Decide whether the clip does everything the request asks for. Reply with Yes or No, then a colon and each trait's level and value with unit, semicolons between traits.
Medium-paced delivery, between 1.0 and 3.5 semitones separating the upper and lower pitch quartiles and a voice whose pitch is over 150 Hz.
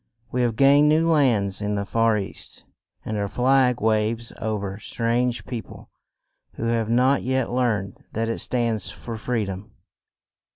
No: average, 165 wpm; average, 2.8 semitones; low, 115 Hz